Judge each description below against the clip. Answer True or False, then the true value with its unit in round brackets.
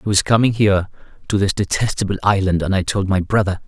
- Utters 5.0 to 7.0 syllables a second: True (6.4 syllables/s)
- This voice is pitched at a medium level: False (100 Hz)